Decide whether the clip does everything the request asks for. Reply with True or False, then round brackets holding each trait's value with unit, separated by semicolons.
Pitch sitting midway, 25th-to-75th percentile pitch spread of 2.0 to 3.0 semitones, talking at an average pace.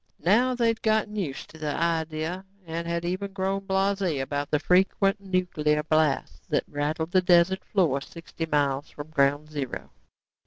False (170 Hz; 4.1 semitones; 160 wpm)